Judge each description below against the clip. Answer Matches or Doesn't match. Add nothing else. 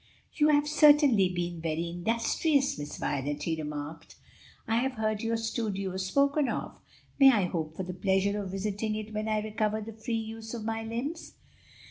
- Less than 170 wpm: Doesn't match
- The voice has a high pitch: Matches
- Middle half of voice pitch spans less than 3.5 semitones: Doesn't match